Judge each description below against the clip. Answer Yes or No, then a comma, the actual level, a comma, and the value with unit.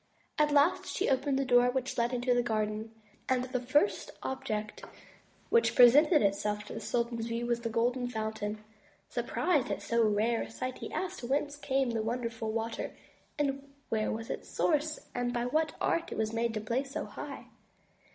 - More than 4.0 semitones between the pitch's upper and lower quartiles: No, average, 3.1 semitones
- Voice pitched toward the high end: Yes, high, 245 Hz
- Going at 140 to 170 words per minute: No, average, 180 wpm